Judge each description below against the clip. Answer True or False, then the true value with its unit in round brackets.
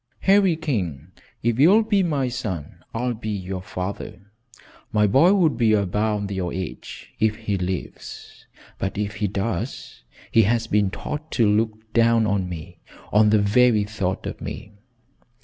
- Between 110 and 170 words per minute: True (155 wpm)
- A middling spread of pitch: True (3.6 semitones)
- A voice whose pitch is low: True (105 Hz)